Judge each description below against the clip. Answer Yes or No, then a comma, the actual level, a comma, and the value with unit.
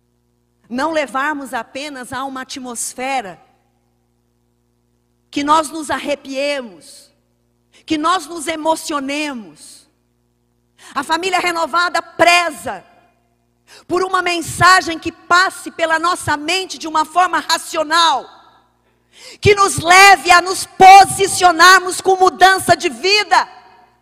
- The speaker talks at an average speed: No, slow, 100 wpm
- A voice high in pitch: Yes, very high, 315 Hz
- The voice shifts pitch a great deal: Yes, wide, 6.1 semitones